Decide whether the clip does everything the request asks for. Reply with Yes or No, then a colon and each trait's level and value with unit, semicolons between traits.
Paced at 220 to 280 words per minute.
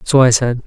Yes: fast, 270 wpm